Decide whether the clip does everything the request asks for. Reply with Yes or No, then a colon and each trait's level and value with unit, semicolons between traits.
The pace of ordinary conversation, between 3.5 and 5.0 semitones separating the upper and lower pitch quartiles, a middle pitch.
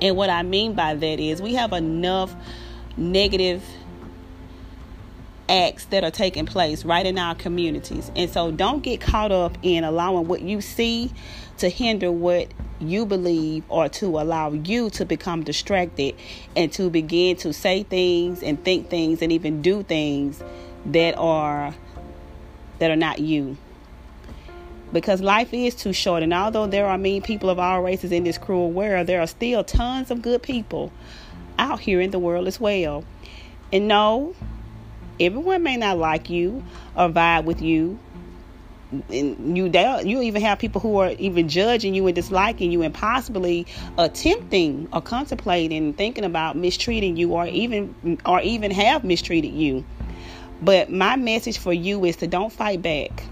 Yes: average, 165 wpm; average, 4.2 semitones; medium, 175 Hz